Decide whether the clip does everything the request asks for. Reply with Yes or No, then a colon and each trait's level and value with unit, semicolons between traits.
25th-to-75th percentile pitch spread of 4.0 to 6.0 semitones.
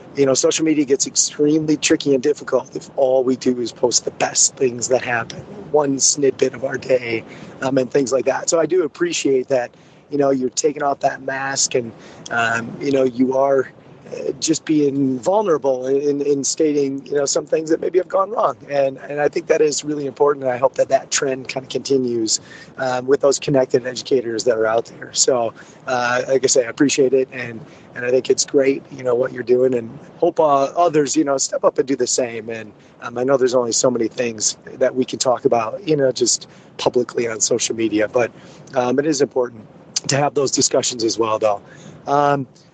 No: average, 3.5 semitones